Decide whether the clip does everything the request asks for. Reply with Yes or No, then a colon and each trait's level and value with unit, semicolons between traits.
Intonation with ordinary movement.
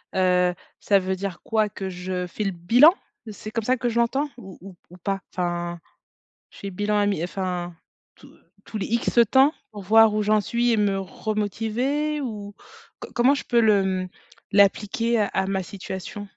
Yes: average, 3.4 semitones